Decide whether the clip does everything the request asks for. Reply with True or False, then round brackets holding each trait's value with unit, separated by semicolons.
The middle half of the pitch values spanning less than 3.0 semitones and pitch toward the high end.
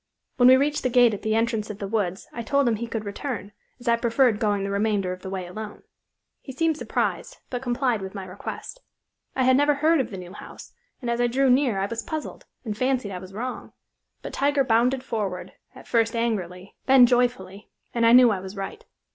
False (4.2 semitones; 230 Hz)